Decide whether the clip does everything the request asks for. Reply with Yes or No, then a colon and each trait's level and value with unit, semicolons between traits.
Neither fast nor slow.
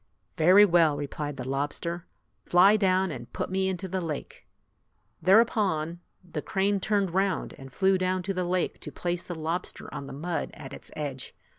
Yes: average, 175 wpm